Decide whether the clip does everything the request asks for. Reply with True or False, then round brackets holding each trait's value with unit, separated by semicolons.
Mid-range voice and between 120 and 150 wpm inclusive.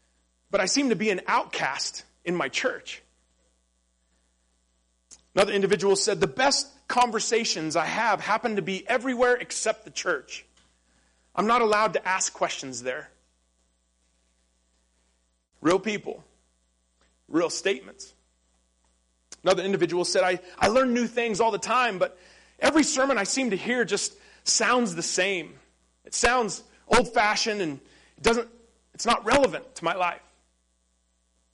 True (180 Hz; 135 wpm)